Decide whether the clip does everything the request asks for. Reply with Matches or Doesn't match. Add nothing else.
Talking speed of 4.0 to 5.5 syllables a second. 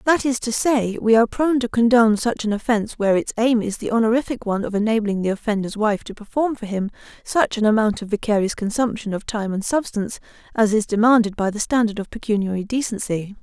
Doesn't match